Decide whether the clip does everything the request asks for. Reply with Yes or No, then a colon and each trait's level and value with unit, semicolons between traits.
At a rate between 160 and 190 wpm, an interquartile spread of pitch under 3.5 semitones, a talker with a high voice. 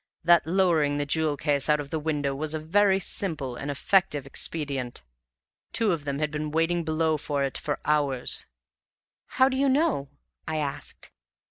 No: average, 170 wpm; average, 3.0 semitones; medium, 155 Hz